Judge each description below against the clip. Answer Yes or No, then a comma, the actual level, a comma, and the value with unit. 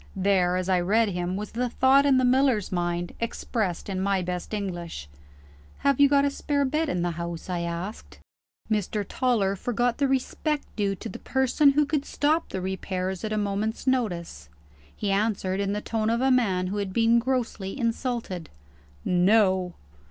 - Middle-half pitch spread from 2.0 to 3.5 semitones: No, wide, 5.5 semitones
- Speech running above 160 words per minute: Yes, average, 180 wpm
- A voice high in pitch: Yes, high, 210 Hz